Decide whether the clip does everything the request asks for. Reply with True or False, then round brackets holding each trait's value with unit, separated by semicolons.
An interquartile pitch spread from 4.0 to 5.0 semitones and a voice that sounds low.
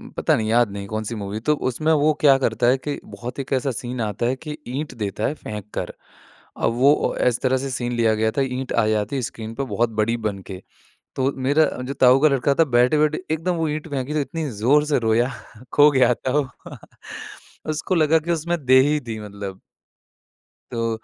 True (4.7 semitones; 130 Hz)